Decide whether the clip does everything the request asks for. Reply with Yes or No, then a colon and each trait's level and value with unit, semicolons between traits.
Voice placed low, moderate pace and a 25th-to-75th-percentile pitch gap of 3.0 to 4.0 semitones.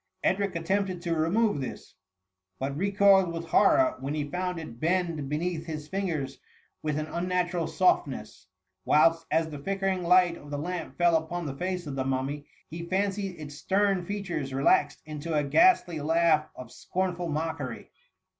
No: medium, 170 Hz; average, 165 wpm; average, 3.5 semitones